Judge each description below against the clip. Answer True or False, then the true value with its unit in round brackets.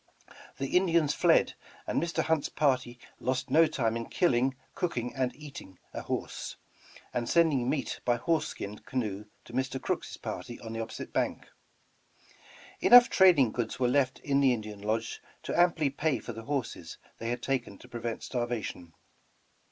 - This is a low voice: True (130 Hz)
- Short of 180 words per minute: True (160 wpm)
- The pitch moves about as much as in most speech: True (3.9 semitones)